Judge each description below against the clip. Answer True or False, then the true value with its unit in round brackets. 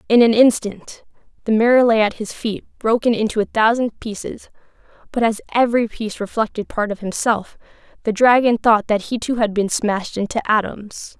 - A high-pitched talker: True (220 Hz)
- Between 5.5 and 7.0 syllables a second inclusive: False (5.3 syllables/s)